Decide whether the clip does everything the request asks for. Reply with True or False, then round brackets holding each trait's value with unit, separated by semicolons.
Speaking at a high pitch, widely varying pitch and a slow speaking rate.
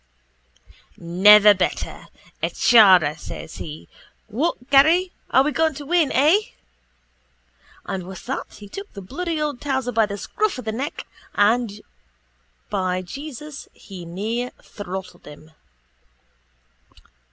True (225 Hz; 7.3 semitones; 125 wpm)